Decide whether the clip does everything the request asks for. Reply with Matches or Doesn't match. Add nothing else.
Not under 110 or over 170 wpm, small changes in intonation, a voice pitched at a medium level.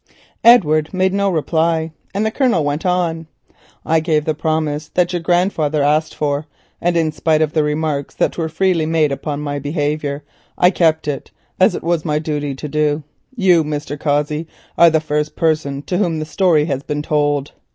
Doesn't match